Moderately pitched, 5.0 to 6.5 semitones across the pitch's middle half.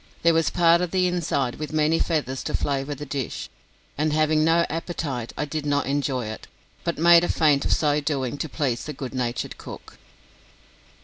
No: medium, 150 Hz; average, 3.2 semitones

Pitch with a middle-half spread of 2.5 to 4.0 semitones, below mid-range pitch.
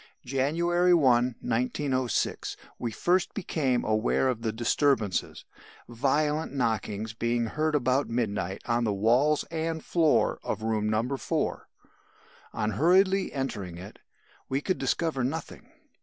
No: average, 5.3 semitones; low, 130 Hz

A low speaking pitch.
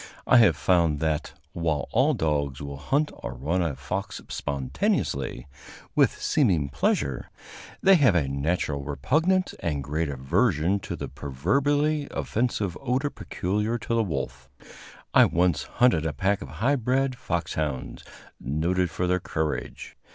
Yes: very low, 85 Hz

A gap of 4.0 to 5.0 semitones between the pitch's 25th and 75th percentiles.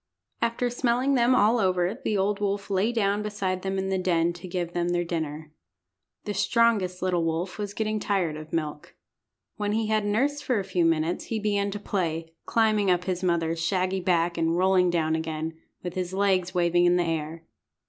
No: average, 3.3 semitones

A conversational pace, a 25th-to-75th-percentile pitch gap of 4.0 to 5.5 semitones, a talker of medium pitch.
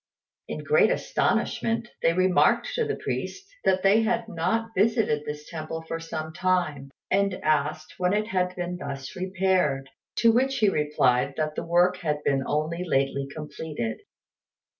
Yes: average, 155 wpm; average, 4.7 semitones; medium, 170 Hz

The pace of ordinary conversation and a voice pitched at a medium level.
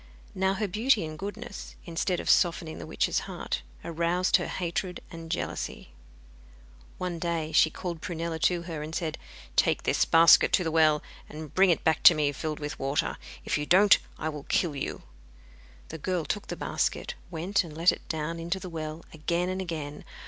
Yes: average, 190 wpm; medium, 165 Hz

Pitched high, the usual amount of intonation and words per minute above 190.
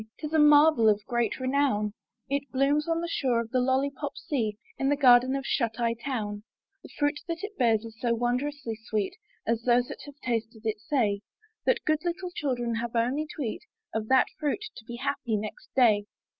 Yes: very high, 250 Hz; average, 4.2 semitones; average, 200 wpm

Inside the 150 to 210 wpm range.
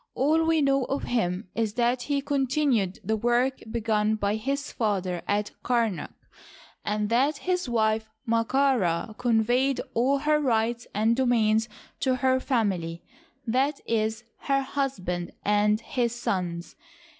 No: average, 140 wpm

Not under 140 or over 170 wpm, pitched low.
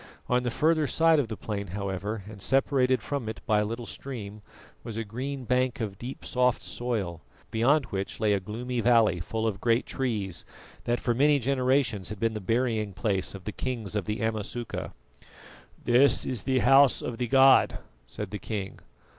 No: average, 185 wpm; low, 115 Hz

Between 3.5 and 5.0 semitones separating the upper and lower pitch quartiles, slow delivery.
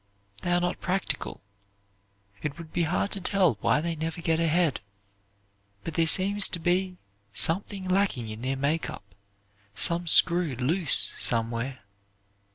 No: average, 4.3 semitones; average, 145 wpm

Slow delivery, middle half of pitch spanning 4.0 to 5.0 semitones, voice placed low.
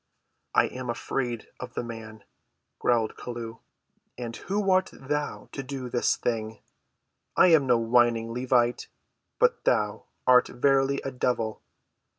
No: slow, 130 wpm; average, 2.8 semitones; low, 125 Hz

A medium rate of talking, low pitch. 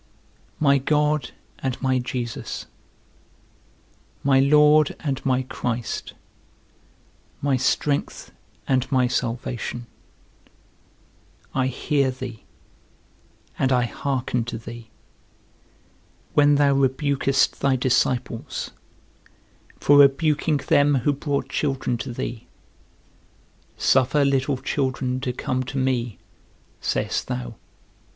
No: slow, 95 wpm; low, 130 Hz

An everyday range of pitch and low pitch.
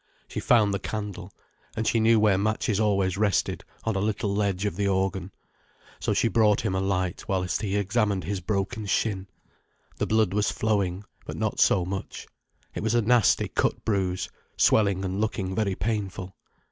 No: narrow, 2.3 semitones; low, 100 Hz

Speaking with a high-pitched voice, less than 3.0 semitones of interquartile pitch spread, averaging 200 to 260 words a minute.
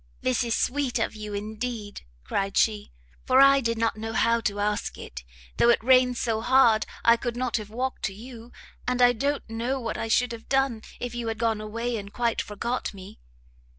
Yes: high, 230 Hz; narrow, 2.4 semitones; fast, 205 wpm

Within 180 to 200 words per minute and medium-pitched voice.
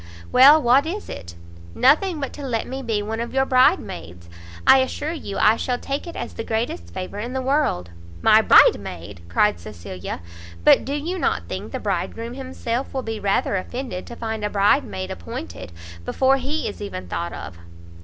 No: average, 190 wpm; high, 230 Hz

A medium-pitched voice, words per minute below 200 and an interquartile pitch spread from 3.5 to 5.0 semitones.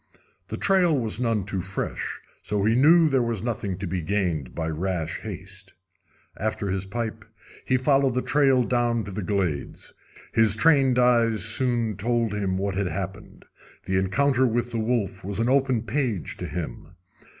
No: low, 110 Hz; average, 170 wpm; average, 4.3 semitones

